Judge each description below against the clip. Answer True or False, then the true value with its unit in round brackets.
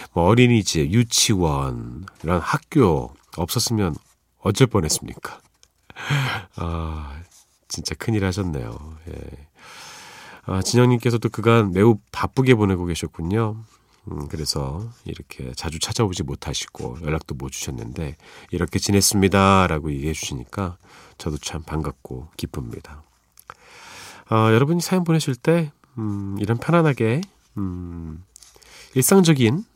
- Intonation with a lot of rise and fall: True (6.6 semitones)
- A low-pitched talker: True (95 Hz)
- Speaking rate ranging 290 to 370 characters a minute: False (260 characters per minute)